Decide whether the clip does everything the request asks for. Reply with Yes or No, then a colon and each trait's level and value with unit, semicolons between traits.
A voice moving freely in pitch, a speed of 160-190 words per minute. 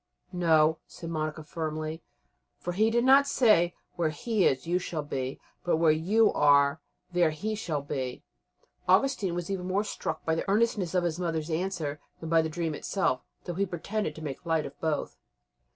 No: average, 3.5 semitones; average, 185 wpm